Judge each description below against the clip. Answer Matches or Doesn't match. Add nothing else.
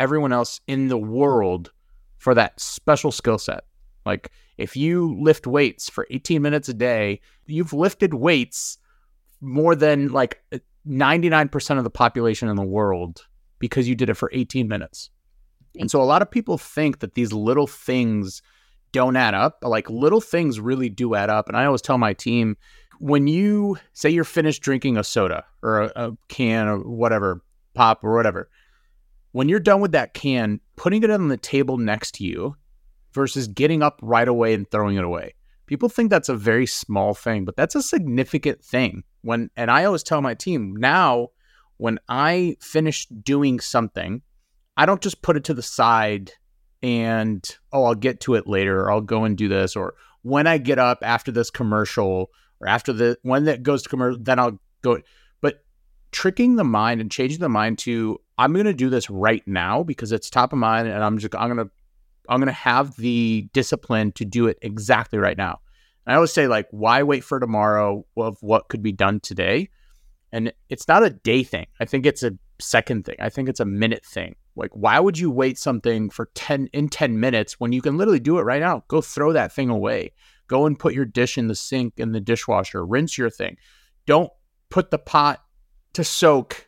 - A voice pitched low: Matches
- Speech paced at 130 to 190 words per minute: Doesn't match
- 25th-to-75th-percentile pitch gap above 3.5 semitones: Matches